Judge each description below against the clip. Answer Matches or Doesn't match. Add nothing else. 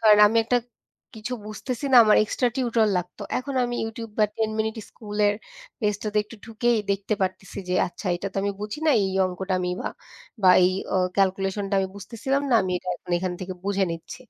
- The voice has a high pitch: Matches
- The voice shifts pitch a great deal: Doesn't match